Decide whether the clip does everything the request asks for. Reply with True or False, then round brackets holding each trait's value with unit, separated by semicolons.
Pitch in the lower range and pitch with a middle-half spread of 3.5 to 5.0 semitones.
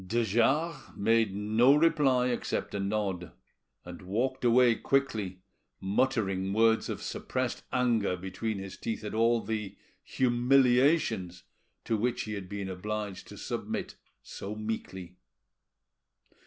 True (110 Hz; 4.0 semitones)